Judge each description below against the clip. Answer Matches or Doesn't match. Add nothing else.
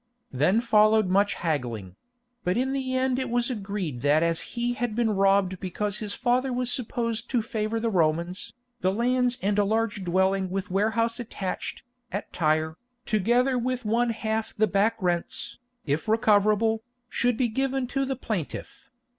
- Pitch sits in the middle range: Doesn't match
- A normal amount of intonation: Matches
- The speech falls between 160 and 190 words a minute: Matches